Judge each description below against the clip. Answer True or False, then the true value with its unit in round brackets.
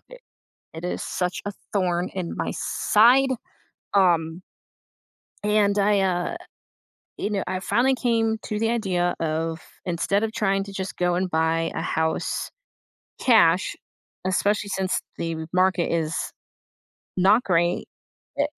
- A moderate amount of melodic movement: True (3.4 semitones)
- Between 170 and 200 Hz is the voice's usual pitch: True (190 Hz)